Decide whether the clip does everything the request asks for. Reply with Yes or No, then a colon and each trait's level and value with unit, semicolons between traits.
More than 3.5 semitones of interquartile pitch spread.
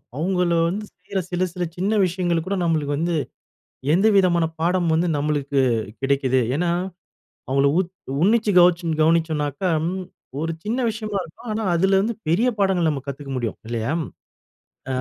Yes: average, 4.4 semitones